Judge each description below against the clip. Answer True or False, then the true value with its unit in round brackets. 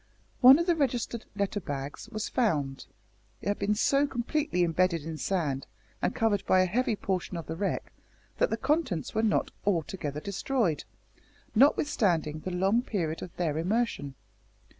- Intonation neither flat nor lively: False (6.1 semitones)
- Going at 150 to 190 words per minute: True (160 wpm)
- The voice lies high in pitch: True (195 Hz)